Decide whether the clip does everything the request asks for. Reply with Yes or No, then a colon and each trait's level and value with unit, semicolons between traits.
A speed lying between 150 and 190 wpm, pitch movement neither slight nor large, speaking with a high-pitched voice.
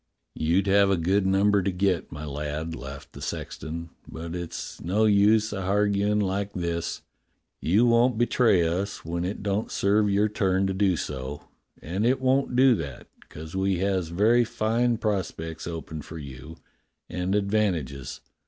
No: average, 160 wpm; average, 3.9 semitones; very low, 95 Hz